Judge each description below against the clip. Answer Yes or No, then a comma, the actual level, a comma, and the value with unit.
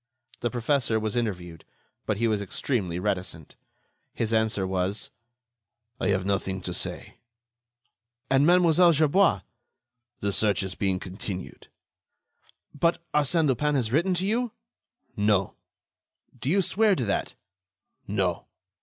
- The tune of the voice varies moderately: No, wide, 7.7 semitones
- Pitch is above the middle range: No, low, 110 Hz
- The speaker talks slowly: Yes, slow, 125 wpm